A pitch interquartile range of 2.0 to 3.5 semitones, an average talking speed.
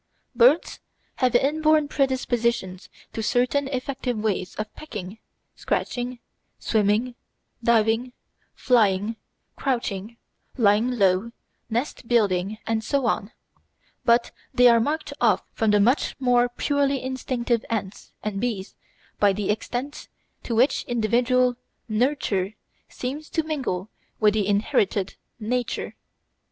No: average, 3.2 semitones; slow, 115 wpm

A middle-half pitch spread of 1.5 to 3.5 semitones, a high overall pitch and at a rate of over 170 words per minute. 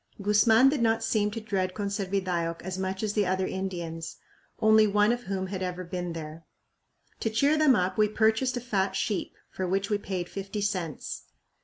Yes: average, 2.9 semitones; high, 195 Hz; average, 185 wpm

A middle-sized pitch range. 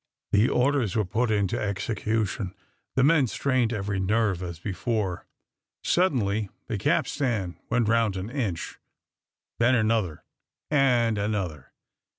Yes: average, 3.7 semitones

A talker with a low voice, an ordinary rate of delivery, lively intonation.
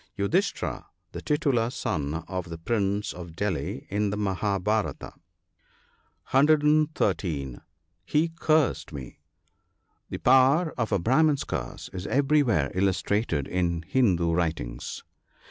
No: low, 100 Hz; slow, 110 wpm; wide, 7.8 semitones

